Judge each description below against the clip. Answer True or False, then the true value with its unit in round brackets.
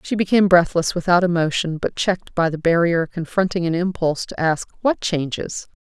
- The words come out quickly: False (175 wpm)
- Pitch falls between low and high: True (175 Hz)